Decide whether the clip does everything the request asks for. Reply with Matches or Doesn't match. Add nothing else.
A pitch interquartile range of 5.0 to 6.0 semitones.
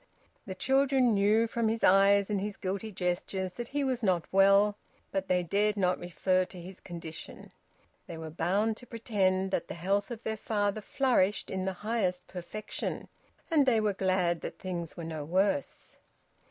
Doesn't match